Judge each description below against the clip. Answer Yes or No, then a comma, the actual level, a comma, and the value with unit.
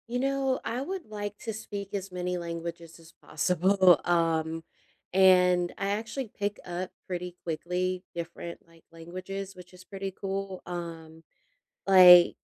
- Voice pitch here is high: No, medium, 180 Hz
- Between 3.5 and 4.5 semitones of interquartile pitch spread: No, narrow, 2.5 semitones